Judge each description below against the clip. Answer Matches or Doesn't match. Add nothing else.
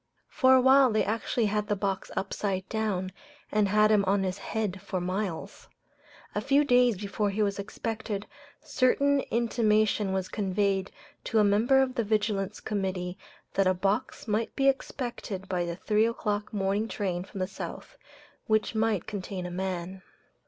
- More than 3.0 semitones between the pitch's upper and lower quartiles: Doesn't match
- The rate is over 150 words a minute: Matches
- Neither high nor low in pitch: Doesn't match